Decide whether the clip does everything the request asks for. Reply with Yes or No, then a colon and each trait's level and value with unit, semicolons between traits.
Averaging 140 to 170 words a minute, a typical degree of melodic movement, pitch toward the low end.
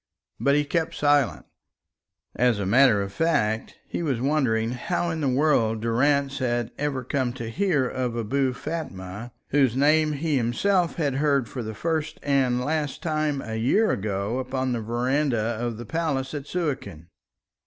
Yes: average, 165 wpm; average, 4.1 semitones; low, 130 Hz